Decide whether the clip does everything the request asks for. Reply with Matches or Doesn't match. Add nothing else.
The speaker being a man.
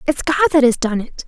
Doesn't match